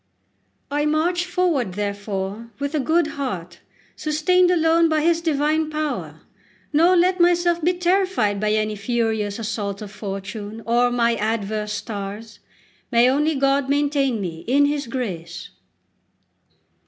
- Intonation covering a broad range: Yes, wide, 7.0 semitones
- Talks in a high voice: Yes, very high, 255 Hz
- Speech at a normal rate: No, slow, 130 wpm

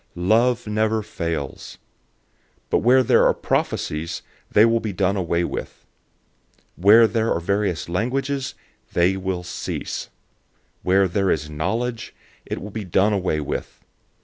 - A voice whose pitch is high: No, low, 100 Hz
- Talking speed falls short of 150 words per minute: Yes, average, 140 wpm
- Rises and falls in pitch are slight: No, average, 4.2 semitones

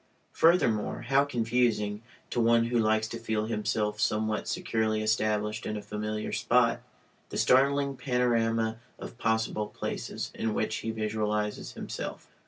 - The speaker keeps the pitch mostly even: Yes, narrow, 1.6 semitones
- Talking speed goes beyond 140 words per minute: No, slow, 135 wpm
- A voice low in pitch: Yes, low, 110 Hz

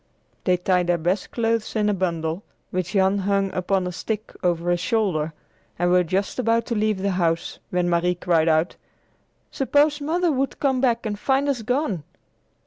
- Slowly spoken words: No, average, 180 wpm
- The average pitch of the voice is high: Yes, high, 195 Hz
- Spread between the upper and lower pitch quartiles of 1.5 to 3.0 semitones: No, average, 4.5 semitones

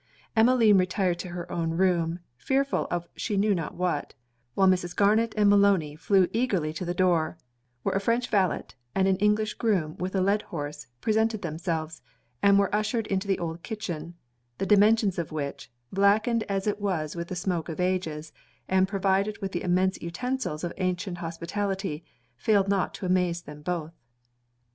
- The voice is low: No, medium, 185 Hz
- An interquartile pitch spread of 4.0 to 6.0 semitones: No, average, 3.2 semitones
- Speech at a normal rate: Yes, average, 170 wpm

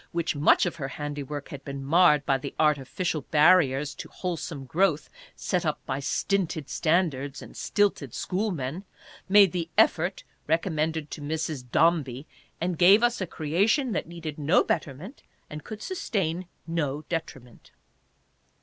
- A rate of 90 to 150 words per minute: Yes, average, 140 wpm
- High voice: No, medium, 160 Hz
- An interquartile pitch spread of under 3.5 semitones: No, average, 3.9 semitones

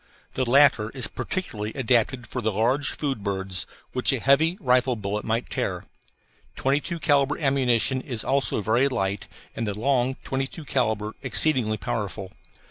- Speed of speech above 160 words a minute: No, average, 150 wpm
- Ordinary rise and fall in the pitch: Yes, average, 4.1 semitones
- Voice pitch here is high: No, low, 125 Hz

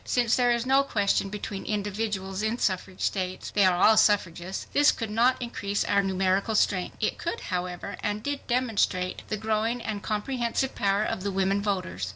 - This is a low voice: No, high, 205 Hz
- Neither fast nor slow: Yes, average, 170 wpm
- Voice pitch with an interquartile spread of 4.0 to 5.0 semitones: No, average, 3.1 semitones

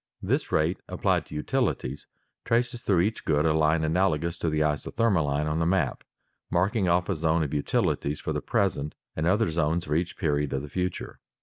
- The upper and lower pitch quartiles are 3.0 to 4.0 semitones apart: Yes, average, 3.4 semitones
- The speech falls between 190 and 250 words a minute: Yes, average, 195 wpm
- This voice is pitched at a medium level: No, very low, 80 Hz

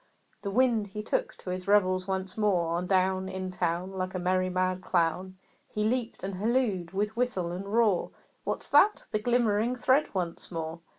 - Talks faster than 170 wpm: Yes, average, 180 wpm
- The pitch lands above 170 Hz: Yes, high, 190 Hz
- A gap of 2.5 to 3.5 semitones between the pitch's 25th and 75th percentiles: Yes, average, 2.9 semitones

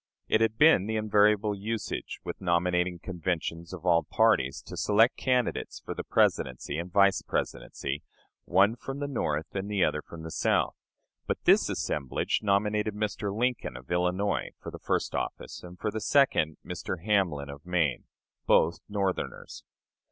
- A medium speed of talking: Yes, average, 160 wpm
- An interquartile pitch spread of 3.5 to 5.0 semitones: Yes, average, 4.0 semitones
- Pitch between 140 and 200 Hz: No, very low, 95 Hz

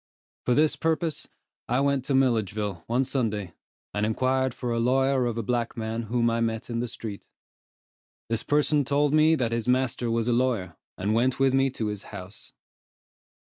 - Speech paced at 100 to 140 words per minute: No, average, 185 wpm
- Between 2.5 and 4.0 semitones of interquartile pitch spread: Yes, average, 3.1 semitones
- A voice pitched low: Yes, low, 120 Hz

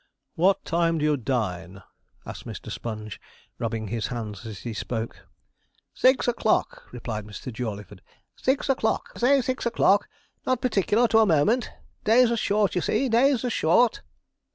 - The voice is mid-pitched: Yes, medium, 165 Hz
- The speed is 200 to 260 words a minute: No, average, 155 wpm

